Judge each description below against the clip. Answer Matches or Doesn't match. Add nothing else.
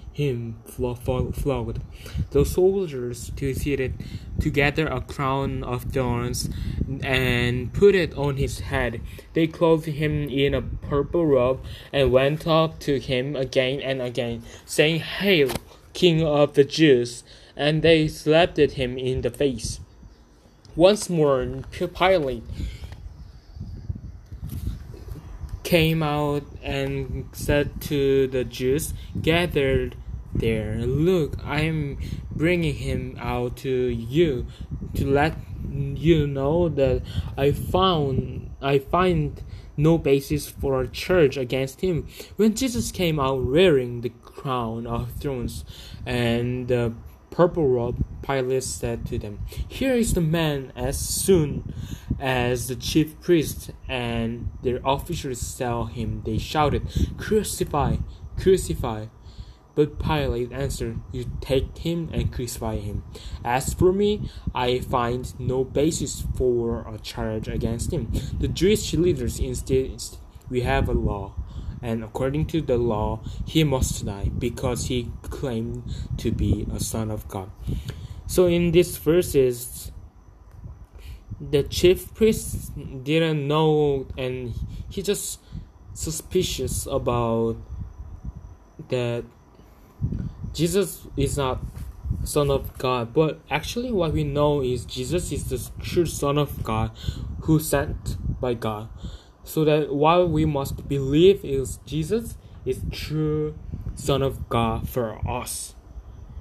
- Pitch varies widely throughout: Doesn't match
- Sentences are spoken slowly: Matches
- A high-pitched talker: Doesn't match